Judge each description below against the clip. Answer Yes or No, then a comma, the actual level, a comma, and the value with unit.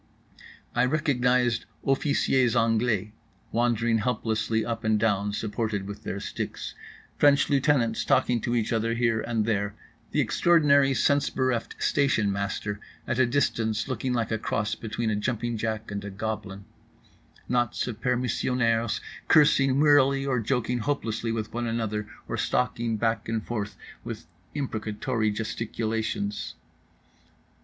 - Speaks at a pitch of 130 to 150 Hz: No, low, 115 Hz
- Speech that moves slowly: Yes, slow, 130 wpm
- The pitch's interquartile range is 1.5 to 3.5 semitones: Yes, narrow, 2.6 semitones